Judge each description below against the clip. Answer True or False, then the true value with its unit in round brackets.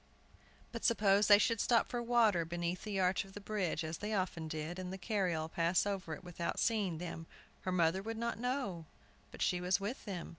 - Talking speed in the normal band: False (210 wpm)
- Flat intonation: False (3.8 semitones)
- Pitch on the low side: False (190 Hz)